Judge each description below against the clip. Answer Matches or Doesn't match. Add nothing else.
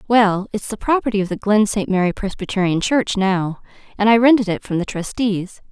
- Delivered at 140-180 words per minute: Doesn't match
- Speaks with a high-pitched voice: Matches